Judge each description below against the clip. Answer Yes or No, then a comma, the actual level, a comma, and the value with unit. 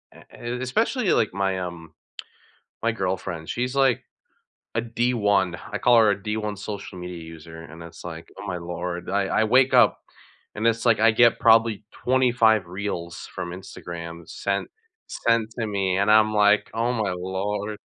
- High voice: No, low, 105 Hz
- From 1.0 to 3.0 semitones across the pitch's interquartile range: No, average, 4.1 semitones